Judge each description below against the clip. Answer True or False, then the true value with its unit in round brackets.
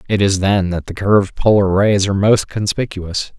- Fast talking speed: False (195 wpm)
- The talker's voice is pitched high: False (100 Hz)